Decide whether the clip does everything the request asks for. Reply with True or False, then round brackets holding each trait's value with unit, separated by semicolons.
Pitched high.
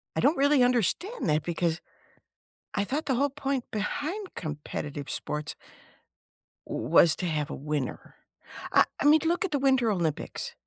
True (240 Hz)